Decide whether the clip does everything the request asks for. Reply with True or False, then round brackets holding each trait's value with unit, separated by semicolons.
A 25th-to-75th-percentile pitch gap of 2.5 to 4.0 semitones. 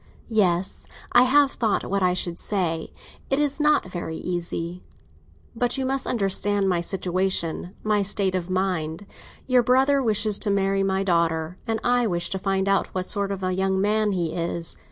True (3.4 semitones)